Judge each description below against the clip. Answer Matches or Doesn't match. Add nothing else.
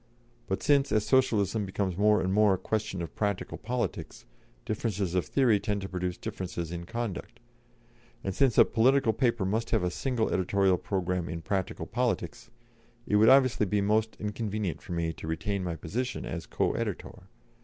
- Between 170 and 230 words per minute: Matches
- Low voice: Matches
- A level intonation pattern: Doesn't match